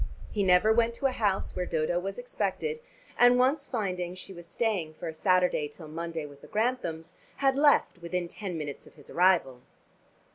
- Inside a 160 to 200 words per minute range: Yes, average, 185 wpm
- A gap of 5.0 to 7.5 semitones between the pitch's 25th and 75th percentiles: Yes, wide, 5.5 semitones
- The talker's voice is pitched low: No, medium, 185 Hz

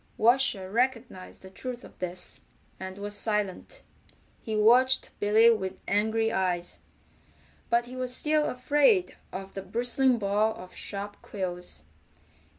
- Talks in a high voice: Yes, high, 220 Hz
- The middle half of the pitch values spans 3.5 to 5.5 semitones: Yes, average, 4.6 semitones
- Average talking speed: No, slow, 130 wpm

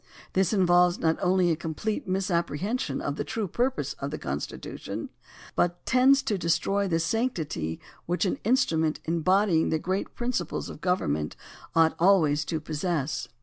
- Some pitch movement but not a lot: Yes, average, 3.9 semitones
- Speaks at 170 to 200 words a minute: No, average, 160 wpm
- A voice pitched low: No, medium, 175 Hz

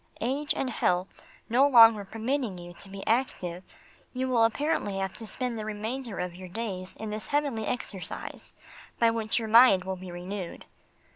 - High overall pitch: Yes, high, 220 Hz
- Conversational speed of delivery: Yes, average, 170 wpm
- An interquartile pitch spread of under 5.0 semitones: Yes, average, 4.5 semitones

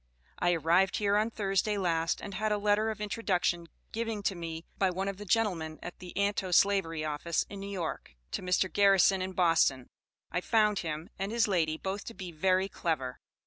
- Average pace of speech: Yes, average, 190 wpm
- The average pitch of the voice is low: No, high, 190 Hz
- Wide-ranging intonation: No, average, 3.2 semitones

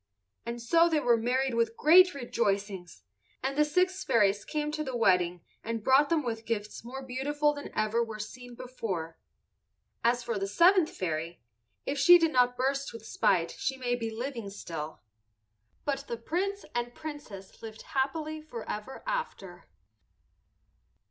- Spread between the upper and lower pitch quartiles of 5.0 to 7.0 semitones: Yes, wide, 5.4 semitones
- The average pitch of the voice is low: No, high, 245 Hz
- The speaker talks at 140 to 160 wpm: Yes, average, 155 wpm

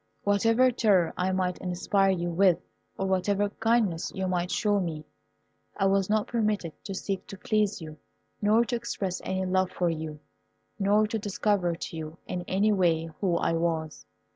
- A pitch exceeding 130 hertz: Yes, high, 190 Hz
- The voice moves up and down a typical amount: Yes, average, 3.1 semitones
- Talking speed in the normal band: Yes, average, 170 wpm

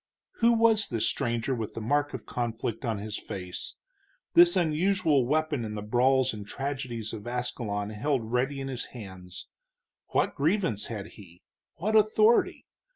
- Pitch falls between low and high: No, low, 125 Hz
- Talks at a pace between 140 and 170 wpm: Yes, average, 155 wpm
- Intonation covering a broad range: Yes, wide, 6.0 semitones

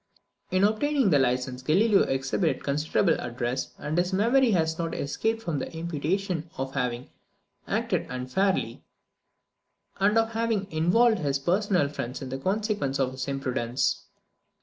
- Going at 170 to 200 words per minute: No, average, 140 wpm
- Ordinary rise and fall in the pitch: No, wide, 7.3 semitones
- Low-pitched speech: No, medium, 160 Hz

